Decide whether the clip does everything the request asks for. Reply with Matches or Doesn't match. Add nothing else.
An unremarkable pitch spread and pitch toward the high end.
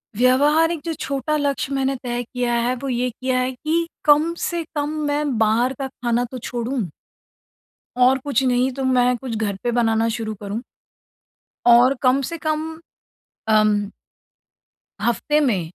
Matches